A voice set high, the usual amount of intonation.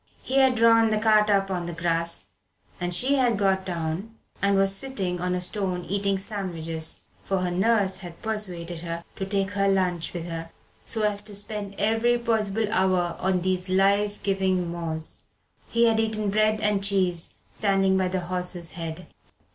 Yes: high, 195 Hz; average, 3.0 semitones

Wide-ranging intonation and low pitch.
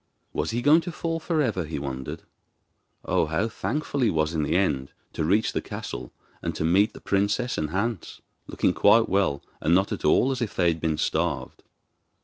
Yes: wide, 7.1 semitones; very low, 95 Hz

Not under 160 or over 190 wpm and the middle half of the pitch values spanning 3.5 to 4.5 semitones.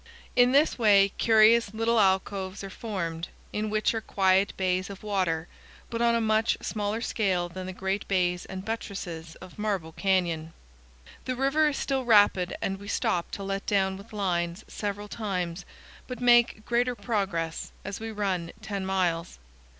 No: average, 165 wpm; average, 3.1 semitones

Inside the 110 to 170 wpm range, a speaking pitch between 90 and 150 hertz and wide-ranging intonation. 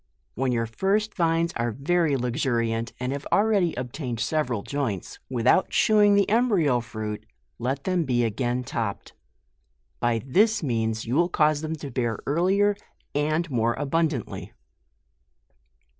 Yes: average, 140 wpm; low, 135 Hz; wide, 6.1 semitones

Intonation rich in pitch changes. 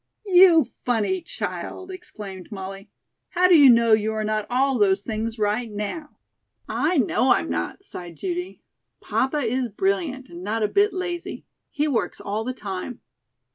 Yes: wide, 8.0 semitones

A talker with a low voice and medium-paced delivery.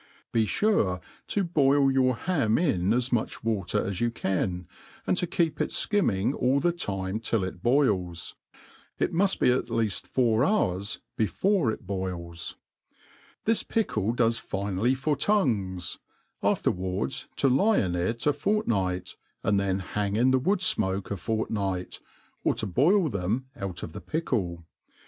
Yes: low, 115 Hz; average, 155 wpm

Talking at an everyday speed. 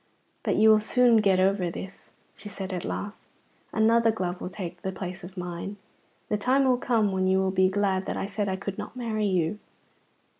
No: fast, 210 wpm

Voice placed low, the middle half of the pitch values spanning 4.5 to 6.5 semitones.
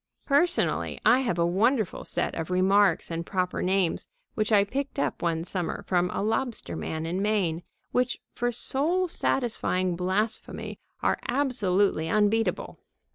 No: high, 200 Hz; average, 5.2 semitones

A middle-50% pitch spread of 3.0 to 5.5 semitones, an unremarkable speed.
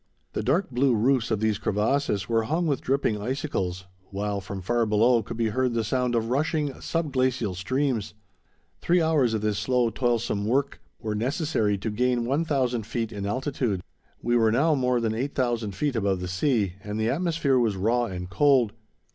Yes: average, 4.2 semitones; average, 180 wpm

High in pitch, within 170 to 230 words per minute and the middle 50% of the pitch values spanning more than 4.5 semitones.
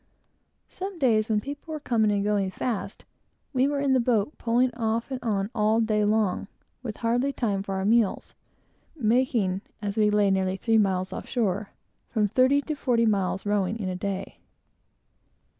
No: high, 220 Hz; average, 175 wpm; average, 3.7 semitones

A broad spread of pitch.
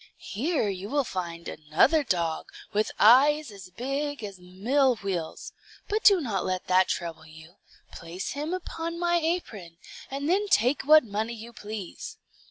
Yes: wide, 8.3 semitones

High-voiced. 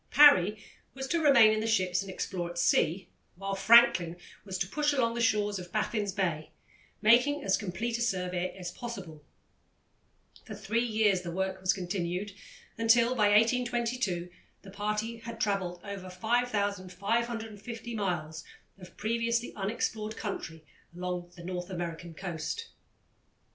Yes: high, 205 Hz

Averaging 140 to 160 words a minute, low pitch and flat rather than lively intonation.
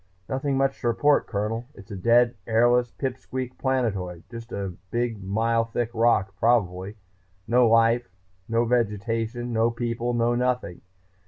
Yes: average, 145 wpm; low, 115 Hz; narrow, 1.7 semitones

